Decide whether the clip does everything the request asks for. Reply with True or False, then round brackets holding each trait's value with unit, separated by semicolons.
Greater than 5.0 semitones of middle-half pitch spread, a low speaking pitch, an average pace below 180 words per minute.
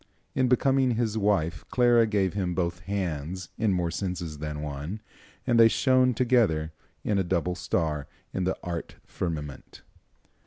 True (5.5 semitones; 95 Hz; 150 wpm)